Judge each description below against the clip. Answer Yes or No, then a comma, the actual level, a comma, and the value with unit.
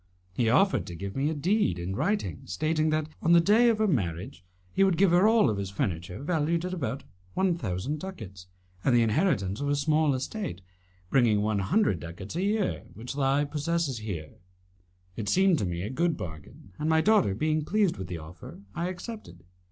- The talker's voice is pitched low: No, medium, 145 Hz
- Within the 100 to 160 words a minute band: No, average, 195 wpm